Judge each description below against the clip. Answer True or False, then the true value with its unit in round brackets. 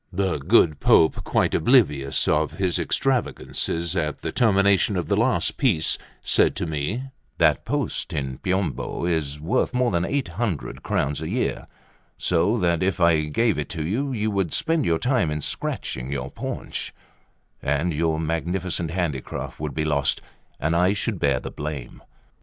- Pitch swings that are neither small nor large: True (4.7 semitones)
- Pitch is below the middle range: True (85 Hz)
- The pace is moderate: True (160 wpm)